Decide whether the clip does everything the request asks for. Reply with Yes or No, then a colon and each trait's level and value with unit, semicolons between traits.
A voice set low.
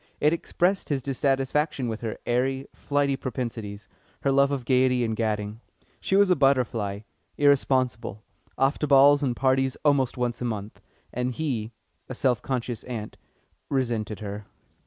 Yes: low, 130 Hz